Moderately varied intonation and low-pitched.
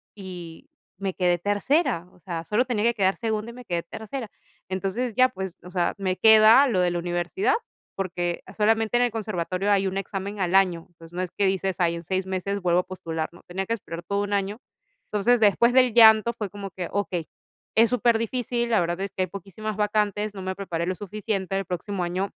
No: average, 3.3 semitones; high, 195 Hz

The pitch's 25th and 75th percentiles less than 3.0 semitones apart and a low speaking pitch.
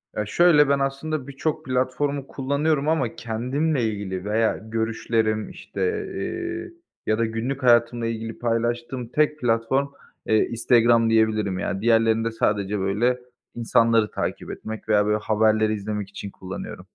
No: average, 3.9 semitones; low, 115 Hz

